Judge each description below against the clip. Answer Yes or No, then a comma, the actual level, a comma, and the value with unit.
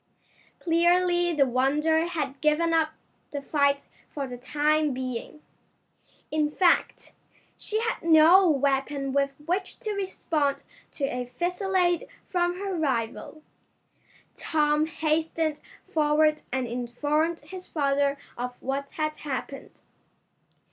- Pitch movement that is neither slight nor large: Yes, average, 3.3 semitones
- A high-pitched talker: Yes, very high, 305 Hz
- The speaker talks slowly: Yes, slow, 115 wpm